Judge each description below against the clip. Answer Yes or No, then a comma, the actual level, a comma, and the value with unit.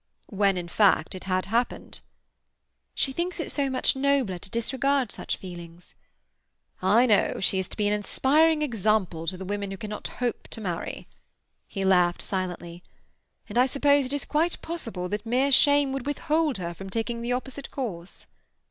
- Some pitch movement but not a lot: No, wide, 6.4 semitones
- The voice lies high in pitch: Yes, high, 225 Hz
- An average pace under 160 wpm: No, average, 175 wpm